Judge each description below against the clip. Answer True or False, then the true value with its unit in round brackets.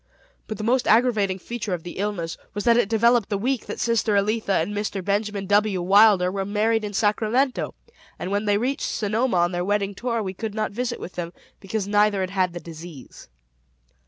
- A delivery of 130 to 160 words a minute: False (200 wpm)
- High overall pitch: True (205 Hz)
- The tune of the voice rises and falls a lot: False (2.7 semitones)